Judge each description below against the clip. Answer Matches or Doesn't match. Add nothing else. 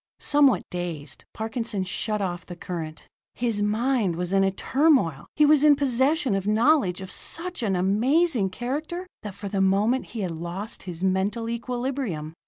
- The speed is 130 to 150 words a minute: Doesn't match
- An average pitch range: Doesn't match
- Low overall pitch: Doesn't match